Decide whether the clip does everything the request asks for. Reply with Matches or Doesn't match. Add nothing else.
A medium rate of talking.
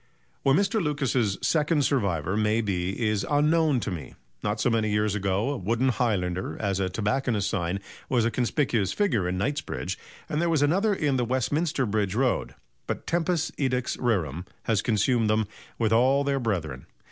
Matches